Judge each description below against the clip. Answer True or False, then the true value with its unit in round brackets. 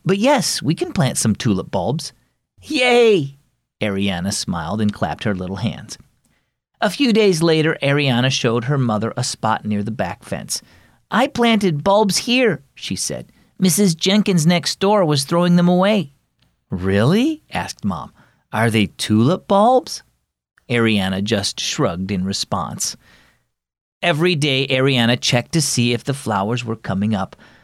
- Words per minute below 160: True (150 wpm)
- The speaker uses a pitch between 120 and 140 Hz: True (135 Hz)